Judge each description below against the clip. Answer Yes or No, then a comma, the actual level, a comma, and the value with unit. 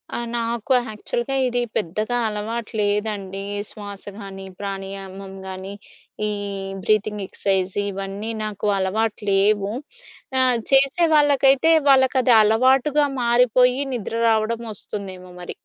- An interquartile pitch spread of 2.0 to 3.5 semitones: No, average, 3.9 semitones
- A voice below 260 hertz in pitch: Yes, high, 215 Hz